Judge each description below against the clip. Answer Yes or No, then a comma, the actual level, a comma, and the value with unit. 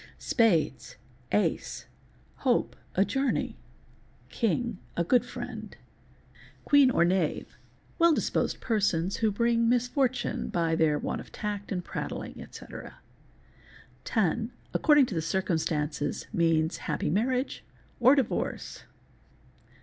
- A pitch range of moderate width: No, wide, 7.1 semitones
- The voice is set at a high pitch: Yes, high, 205 Hz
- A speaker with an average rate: No, slow, 100 wpm